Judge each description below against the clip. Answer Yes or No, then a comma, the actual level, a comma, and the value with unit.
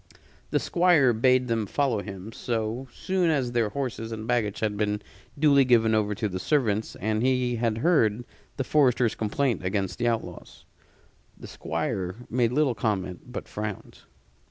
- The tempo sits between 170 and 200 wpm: No, average, 155 wpm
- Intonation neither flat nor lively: Yes, average, 3.3 semitones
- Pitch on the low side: Yes, low, 115 Hz